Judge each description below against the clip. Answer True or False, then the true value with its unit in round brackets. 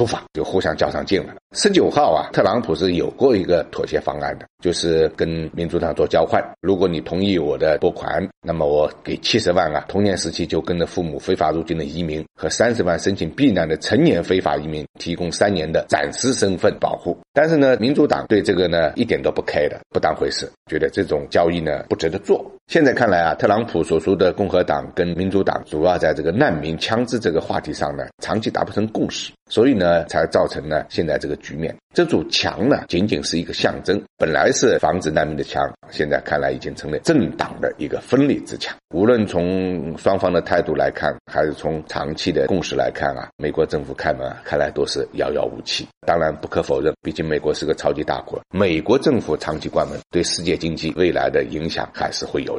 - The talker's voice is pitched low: True (90 Hz)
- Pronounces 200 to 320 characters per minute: False (330 characters per minute)